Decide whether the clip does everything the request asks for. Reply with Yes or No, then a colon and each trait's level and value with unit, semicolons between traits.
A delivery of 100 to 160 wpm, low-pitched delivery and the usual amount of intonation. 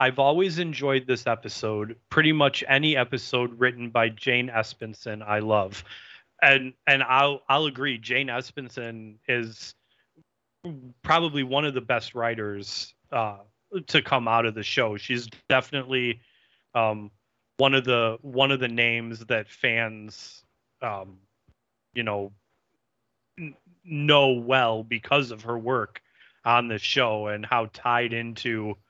Yes: slow, 135 wpm; low, 120 Hz; average, 3.4 semitones